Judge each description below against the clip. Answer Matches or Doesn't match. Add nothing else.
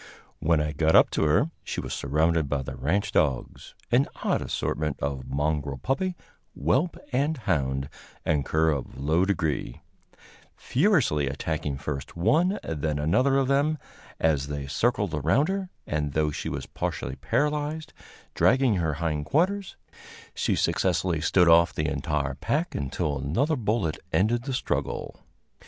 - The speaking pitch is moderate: Doesn't match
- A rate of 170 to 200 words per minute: Doesn't match